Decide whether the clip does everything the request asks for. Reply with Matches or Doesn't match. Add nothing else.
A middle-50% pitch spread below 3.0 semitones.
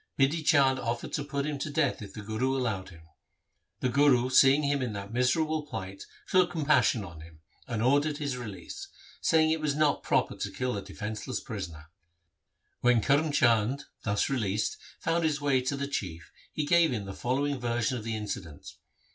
Doesn't match